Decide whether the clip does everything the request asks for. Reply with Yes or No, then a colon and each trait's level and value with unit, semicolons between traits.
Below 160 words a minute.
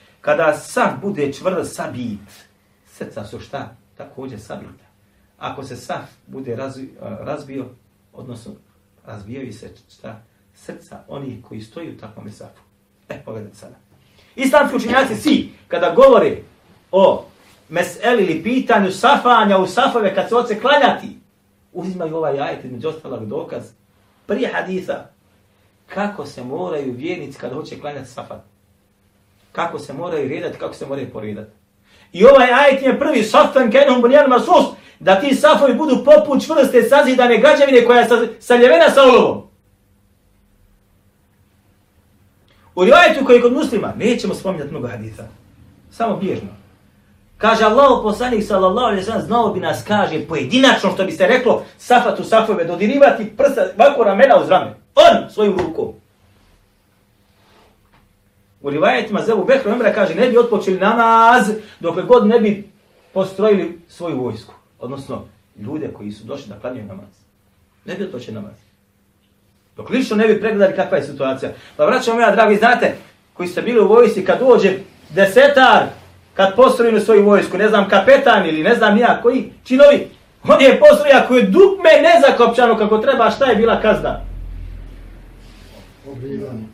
Yes: average, 145 wpm